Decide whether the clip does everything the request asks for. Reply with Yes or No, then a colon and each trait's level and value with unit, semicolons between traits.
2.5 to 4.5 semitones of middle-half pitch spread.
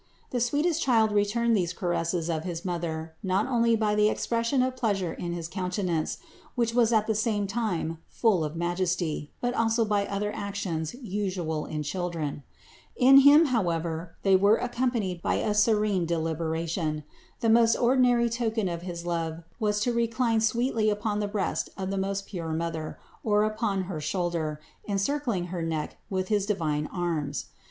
No: average, 5.1 semitones